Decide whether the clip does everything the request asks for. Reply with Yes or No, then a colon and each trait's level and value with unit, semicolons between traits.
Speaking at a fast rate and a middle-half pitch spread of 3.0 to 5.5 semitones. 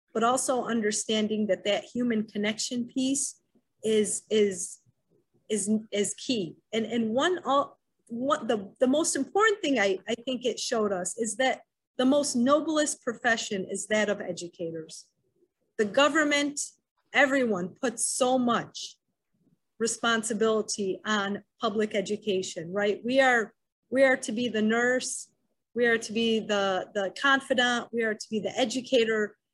No: average, 145 wpm; average, 3.7 semitones